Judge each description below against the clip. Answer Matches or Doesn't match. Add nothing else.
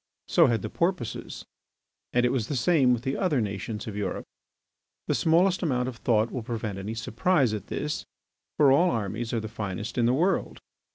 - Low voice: Matches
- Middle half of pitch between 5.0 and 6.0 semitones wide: Matches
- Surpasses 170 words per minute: Matches